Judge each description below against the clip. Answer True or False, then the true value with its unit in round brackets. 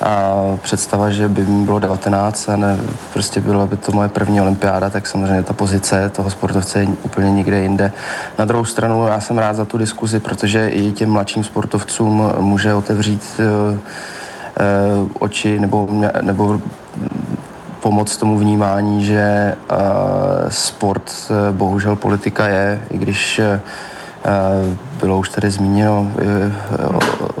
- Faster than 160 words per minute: False (145 wpm)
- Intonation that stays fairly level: True (1.1 semitones)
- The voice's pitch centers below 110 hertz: True (100 Hz)